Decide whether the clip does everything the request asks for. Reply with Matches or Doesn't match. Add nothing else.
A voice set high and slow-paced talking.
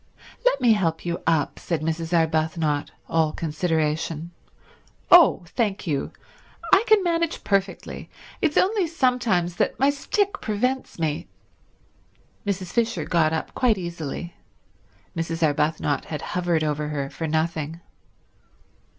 Doesn't match